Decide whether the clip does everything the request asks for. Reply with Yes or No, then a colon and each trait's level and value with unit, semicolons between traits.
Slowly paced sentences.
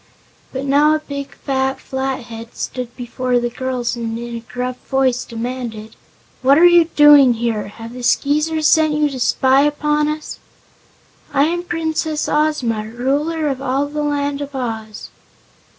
No: average, 155 wpm